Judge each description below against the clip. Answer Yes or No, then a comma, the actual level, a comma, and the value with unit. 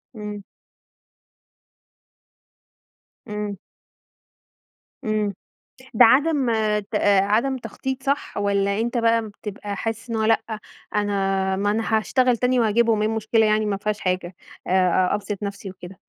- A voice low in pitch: No, high, 215 Hz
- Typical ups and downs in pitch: No, narrow, 2.2 semitones